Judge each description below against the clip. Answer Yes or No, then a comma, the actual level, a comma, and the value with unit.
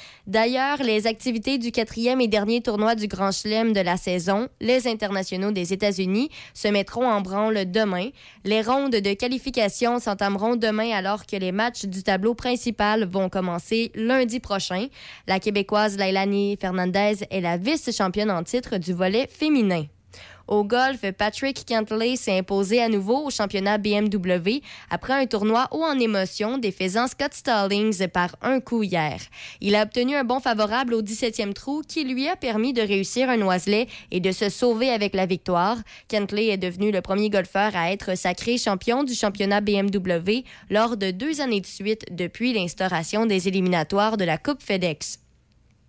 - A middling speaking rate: Yes, average, 165 wpm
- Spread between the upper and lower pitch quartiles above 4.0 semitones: No, average, 3.6 semitones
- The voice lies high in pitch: Yes, high, 210 Hz